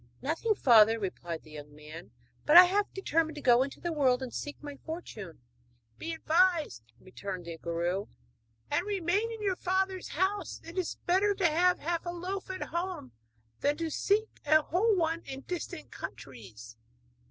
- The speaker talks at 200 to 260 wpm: No, average, 170 wpm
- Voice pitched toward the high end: Yes, very high, 320 Hz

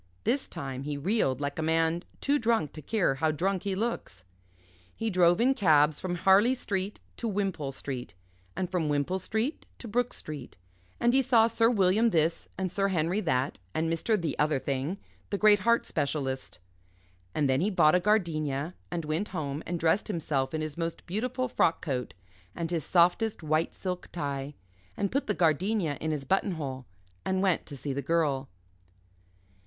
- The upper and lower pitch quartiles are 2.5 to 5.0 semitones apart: No, wide, 5.6 semitones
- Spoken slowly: No, average, 180 wpm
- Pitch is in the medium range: Yes, medium, 170 Hz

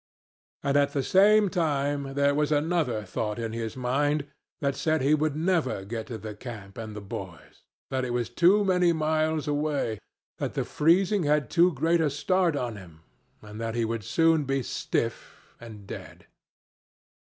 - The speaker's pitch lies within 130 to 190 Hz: Yes, medium, 140 Hz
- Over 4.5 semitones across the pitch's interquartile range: Yes, wide, 5.6 semitones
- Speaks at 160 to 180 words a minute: Yes, average, 175 wpm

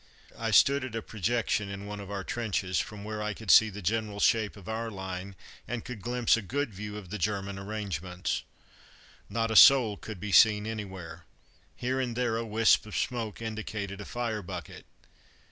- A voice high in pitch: No, low, 105 Hz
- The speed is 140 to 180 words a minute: No, average, 190 wpm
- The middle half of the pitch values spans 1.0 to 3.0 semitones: Yes, narrow, 2.5 semitones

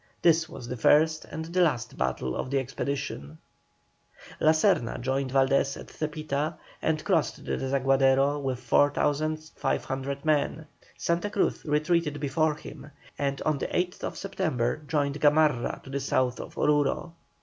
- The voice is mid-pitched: Yes, medium, 145 Hz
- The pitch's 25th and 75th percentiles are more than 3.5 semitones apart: No, average, 2.7 semitones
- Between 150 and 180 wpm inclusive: No, average, 140 wpm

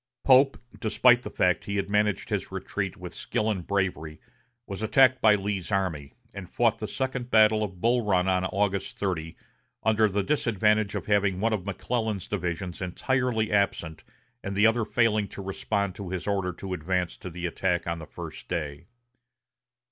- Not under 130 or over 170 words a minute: No, average, 180 wpm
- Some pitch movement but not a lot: Yes, average, 3.1 semitones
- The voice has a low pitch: Yes, low, 100 Hz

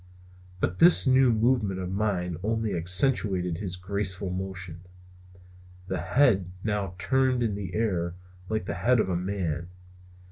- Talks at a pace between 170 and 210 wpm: No, average, 140 wpm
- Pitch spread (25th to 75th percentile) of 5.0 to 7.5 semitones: No, average, 3.7 semitones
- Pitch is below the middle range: Yes, very low, 95 Hz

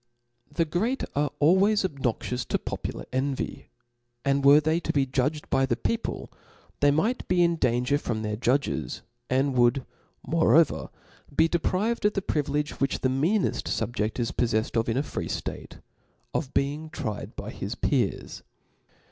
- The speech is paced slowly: No, average, 165 wpm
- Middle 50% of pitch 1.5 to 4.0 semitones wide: No, average, 4.5 semitones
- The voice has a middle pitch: Yes, medium, 145 Hz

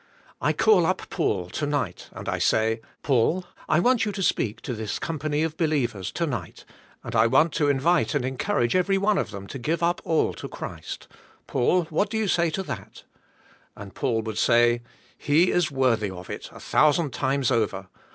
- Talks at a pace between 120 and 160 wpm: No, average, 200 wpm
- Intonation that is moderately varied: No, wide, 6.8 semitones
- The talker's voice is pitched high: No, medium, 145 Hz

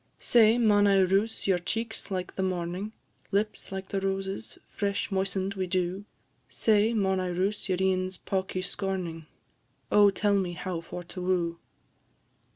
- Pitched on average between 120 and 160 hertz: No, high, 190 Hz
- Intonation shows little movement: Yes, narrow, 1.6 semitones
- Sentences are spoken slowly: No, average, 155 wpm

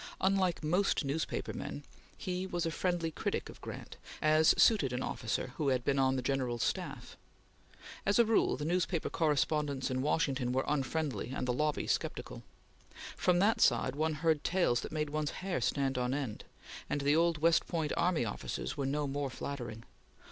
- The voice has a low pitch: No, medium, 150 Hz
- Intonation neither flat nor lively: Yes, average, 3.9 semitones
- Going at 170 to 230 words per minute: Yes, average, 175 wpm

